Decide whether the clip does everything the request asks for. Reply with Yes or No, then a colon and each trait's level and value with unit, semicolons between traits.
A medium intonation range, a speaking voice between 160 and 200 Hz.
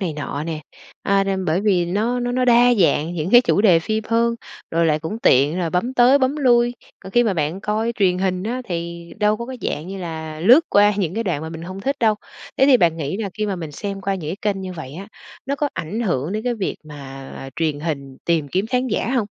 No: wide, 5.9 semitones; high, 190 Hz